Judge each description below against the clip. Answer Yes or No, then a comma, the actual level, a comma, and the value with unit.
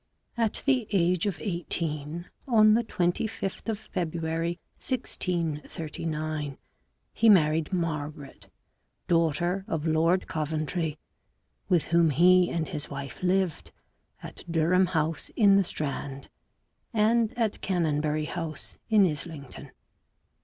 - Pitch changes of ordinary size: Yes, average, 3.6 semitones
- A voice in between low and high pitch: Yes, medium, 170 Hz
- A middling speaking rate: No, slow, 110 wpm